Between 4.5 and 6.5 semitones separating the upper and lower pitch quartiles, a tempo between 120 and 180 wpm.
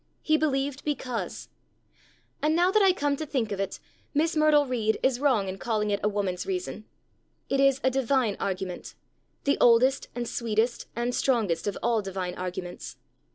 Yes: wide, 5.6 semitones; average, 170 wpm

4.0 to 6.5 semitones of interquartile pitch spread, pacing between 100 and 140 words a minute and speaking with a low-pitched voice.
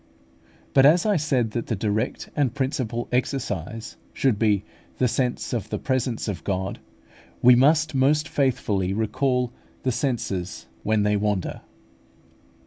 Yes: average, 4.4 semitones; slow, 135 wpm; low, 120 Hz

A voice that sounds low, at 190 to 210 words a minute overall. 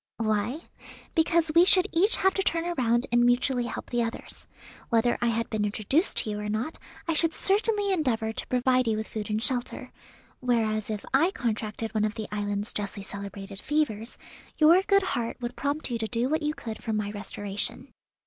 No: high, 240 Hz; average, 195 wpm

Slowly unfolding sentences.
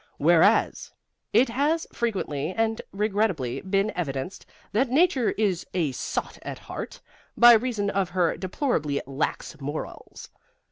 Yes: slow, 125 wpm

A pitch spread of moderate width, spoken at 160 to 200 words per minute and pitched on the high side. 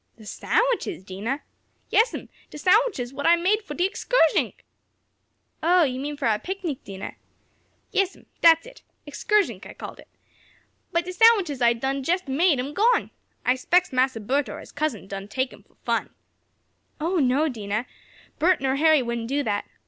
No: wide, 6.4 semitones; average, 170 wpm; very high, 290 Hz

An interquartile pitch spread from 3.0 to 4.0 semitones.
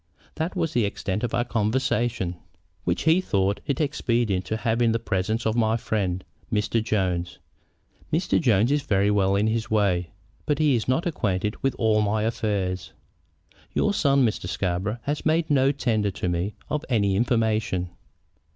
No: average, 4.6 semitones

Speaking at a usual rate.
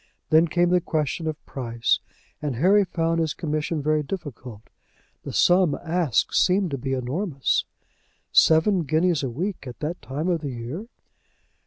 Yes: average, 155 wpm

